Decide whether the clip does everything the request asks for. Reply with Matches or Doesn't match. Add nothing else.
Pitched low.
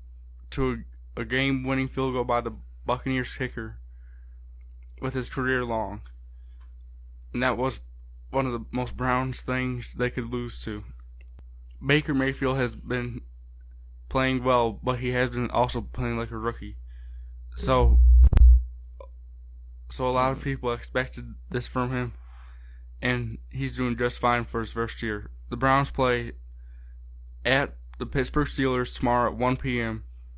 Matches